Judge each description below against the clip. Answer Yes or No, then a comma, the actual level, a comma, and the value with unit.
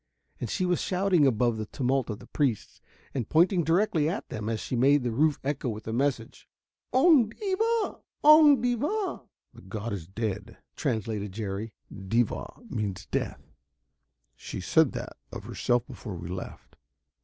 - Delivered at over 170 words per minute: No, average, 155 wpm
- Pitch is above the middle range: No, low, 125 Hz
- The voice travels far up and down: Yes, wide, 9.0 semitones